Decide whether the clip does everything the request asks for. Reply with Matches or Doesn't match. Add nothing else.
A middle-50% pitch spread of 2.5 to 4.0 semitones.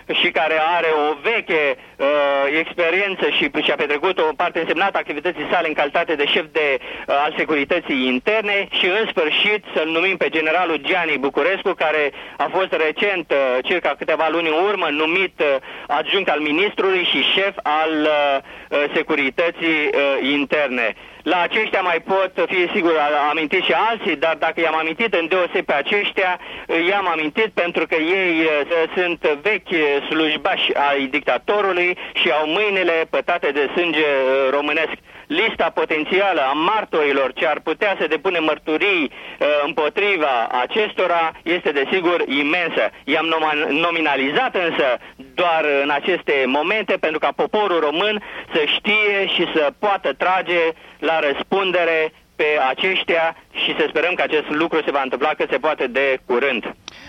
Doesn't match